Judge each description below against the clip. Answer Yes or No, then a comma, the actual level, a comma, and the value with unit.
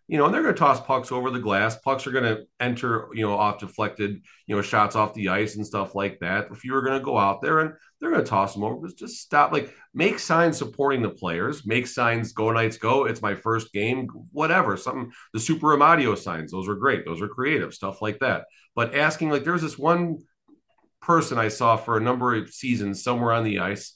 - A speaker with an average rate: No, fast, 240 wpm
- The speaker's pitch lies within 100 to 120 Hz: Yes, low, 115 Hz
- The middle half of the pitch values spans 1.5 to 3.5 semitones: No, average, 4.4 semitones